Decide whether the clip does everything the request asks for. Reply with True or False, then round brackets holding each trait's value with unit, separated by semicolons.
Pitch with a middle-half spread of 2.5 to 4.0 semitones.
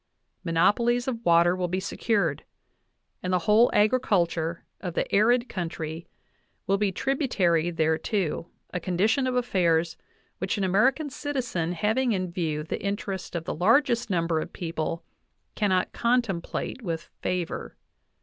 False (5.4 semitones)